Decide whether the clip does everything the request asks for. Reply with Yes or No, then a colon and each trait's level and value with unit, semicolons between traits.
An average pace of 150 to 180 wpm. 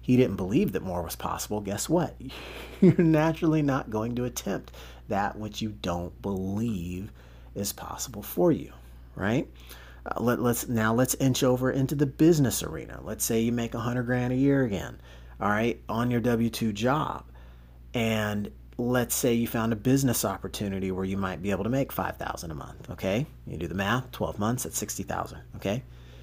No: average, 190 wpm